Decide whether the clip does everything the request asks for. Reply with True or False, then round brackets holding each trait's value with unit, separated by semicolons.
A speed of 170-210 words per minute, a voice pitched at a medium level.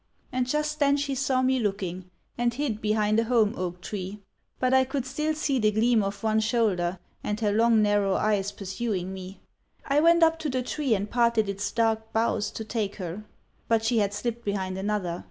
False (200 wpm; 220 Hz)